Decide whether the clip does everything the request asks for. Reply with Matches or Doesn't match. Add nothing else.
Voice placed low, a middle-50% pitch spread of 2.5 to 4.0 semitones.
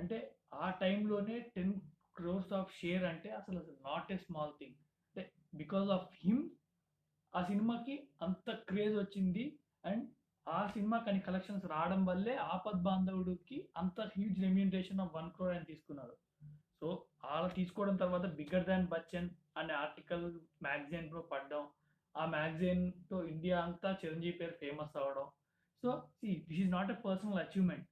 Doesn't match